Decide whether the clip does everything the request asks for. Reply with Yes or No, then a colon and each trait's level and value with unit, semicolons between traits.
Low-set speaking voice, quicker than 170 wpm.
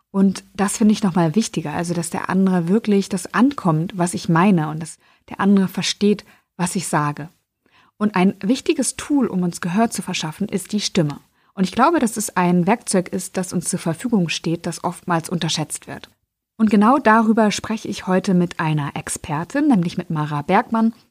No: high, 190 Hz; fast, 190 wpm